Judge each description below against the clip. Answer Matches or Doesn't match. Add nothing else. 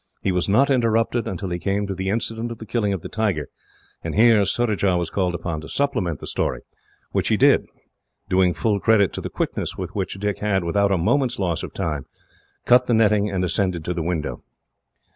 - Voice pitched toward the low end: Matches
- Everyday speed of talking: Doesn't match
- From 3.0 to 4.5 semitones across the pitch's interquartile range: Matches